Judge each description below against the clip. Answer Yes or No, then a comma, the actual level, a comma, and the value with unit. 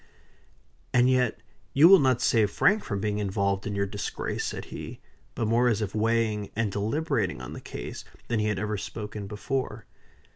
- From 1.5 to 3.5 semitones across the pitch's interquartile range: Yes, average, 3.1 semitones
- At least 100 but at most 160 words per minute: No, average, 180 wpm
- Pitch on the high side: No, low, 110 Hz